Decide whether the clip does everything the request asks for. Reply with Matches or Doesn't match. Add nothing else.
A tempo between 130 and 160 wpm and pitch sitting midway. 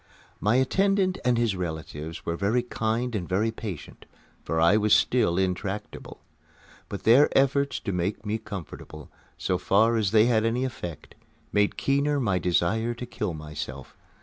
Doesn't match